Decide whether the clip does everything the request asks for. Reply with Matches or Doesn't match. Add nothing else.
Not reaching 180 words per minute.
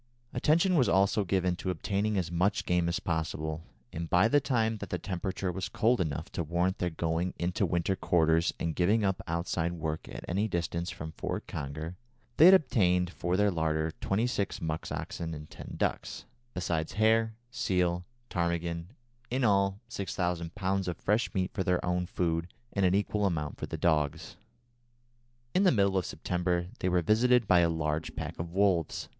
Doesn't match